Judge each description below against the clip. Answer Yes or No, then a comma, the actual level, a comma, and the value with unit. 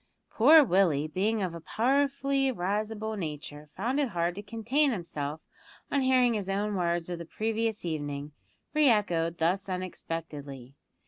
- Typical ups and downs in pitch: No, wide, 5.7 semitones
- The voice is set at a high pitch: Yes, high, 195 Hz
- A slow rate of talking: No, average, 145 wpm